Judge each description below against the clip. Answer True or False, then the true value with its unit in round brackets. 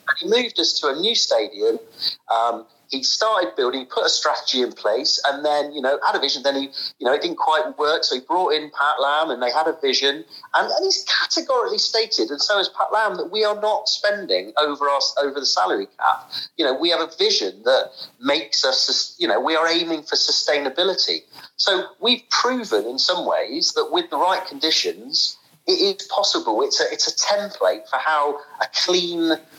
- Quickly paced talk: True (210 wpm)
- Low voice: False (180 Hz)